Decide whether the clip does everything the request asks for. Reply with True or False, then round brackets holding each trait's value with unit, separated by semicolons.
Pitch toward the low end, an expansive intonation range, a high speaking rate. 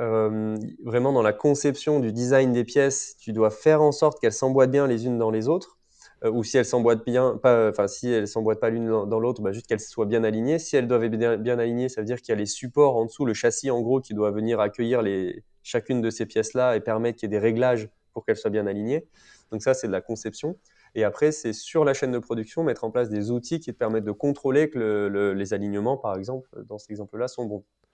False (115 Hz; 2.8 semitones; 260 wpm)